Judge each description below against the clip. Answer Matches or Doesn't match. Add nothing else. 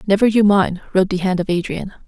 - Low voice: Doesn't match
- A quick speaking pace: Matches